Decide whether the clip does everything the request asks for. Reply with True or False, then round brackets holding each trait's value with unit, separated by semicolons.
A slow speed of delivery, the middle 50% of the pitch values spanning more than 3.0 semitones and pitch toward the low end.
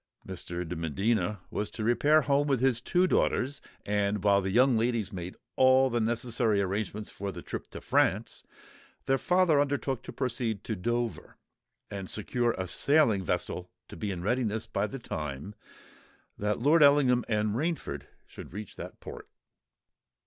False (160 wpm; 4.7 semitones; 110 Hz)